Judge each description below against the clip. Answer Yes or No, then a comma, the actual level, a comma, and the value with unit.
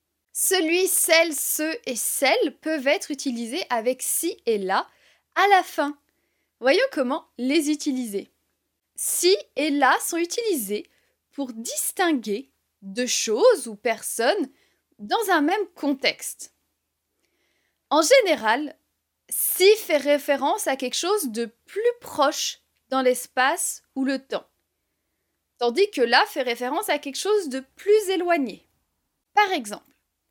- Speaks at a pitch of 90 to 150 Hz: No, very high, 300 Hz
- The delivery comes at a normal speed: No, slow, 125 wpm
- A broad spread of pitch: Yes, wide, 6.3 semitones